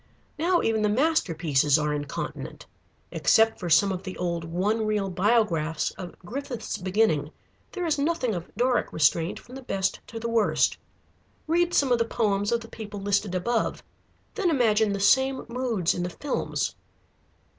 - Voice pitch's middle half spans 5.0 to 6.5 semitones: Yes, wide, 5.4 semitones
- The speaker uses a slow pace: No, average, 165 wpm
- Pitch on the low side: No, high, 215 Hz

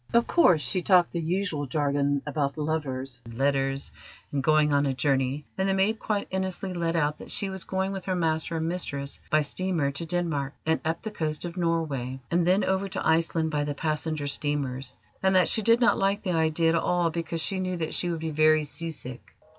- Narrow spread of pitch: No, average, 4.0 semitones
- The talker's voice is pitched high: No, medium, 160 Hz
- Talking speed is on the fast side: Yes, fast, 215 wpm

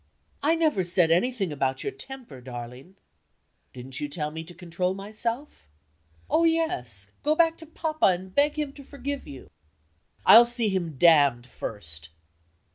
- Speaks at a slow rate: No, average, 150 wpm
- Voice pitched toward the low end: No, medium, 185 Hz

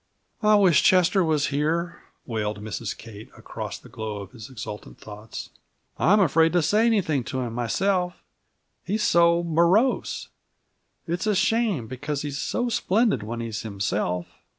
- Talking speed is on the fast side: No, average, 150 wpm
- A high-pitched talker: No, medium, 155 Hz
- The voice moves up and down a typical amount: No, wide, 8.8 semitones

